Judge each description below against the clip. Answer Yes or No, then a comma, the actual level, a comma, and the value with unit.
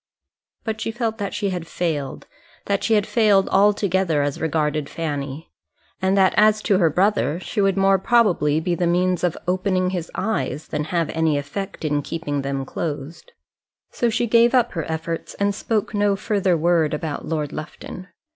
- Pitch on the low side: No, medium, 180 Hz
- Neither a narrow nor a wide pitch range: Yes, average, 4.5 semitones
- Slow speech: No, average, 175 wpm